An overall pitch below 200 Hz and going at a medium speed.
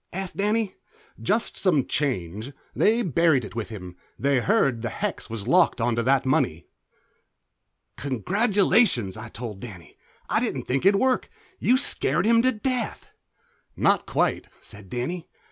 Yes: medium, 140 Hz; average, 145 wpm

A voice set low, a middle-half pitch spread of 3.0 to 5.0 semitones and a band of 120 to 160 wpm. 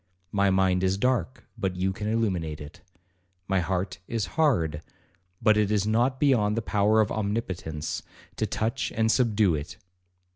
Yes: low, 105 Hz; average, 3.3 semitones; average, 155 wpm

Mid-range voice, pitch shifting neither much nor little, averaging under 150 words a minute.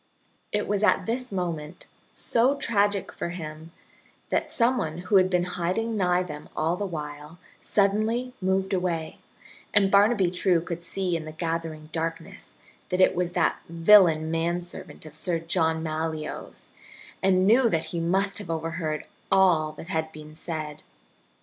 No: medium, 175 Hz; average, 3.3 semitones; average, 155 wpm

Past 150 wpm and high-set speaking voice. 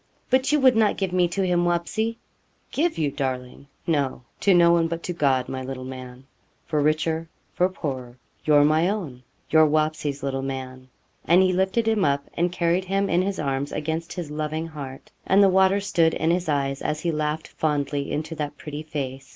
No: average, 195 wpm; medium, 155 Hz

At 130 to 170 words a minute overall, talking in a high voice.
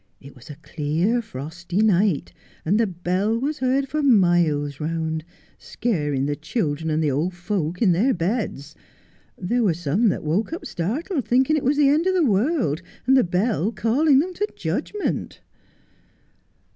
Yes: average, 165 wpm; high, 195 Hz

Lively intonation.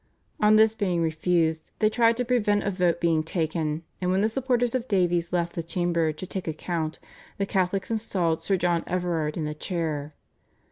No: average, 4.0 semitones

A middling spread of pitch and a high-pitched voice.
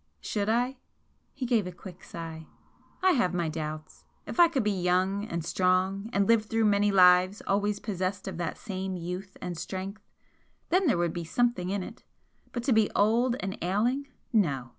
Yes: average, 3.6 semitones; high, 195 Hz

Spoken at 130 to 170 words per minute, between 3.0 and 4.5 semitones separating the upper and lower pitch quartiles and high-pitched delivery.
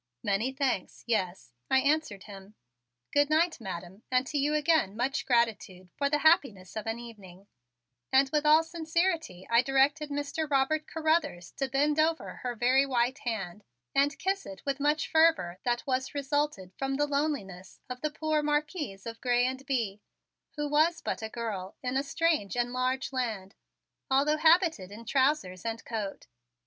No: average, 165 wpm; wide, 5.4 semitones; very high, 265 Hz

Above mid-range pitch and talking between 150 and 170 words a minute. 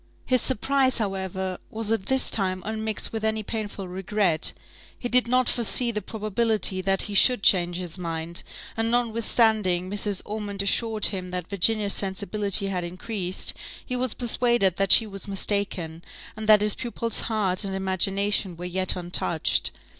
Yes: high, 200 Hz; average, 155 wpm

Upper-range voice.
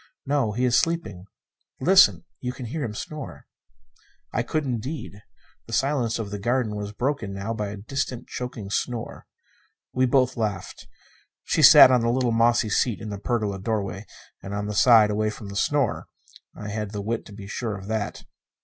No: low, 110 Hz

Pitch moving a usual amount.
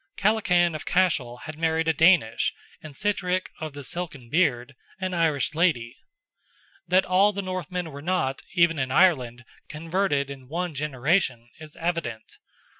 Yes: average, 4.8 semitones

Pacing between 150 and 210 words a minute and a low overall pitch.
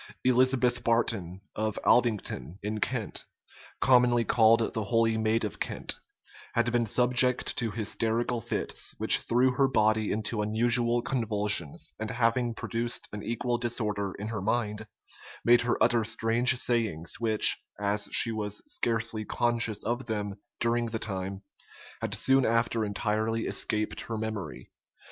No: average, 140 wpm; low, 115 Hz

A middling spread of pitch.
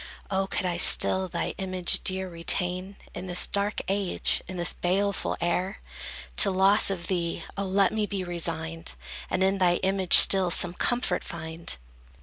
No: narrow, 1.9 semitones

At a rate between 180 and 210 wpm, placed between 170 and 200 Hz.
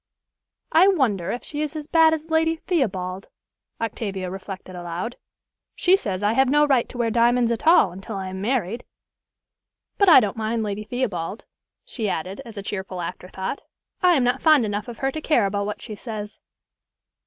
No: average, 185 wpm; high, 225 Hz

